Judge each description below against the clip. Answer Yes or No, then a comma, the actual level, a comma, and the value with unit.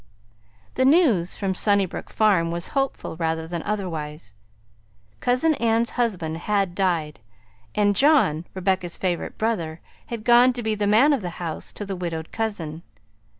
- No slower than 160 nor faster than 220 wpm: No, average, 150 wpm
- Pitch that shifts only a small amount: No, average, 5.3 semitones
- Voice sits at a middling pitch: No, high, 195 Hz